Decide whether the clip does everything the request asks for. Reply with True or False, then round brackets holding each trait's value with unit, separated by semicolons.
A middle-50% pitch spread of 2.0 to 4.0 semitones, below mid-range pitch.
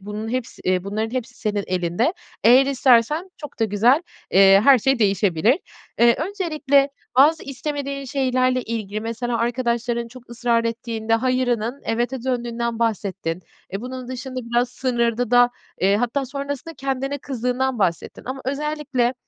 False (2.9 semitones; 245 Hz)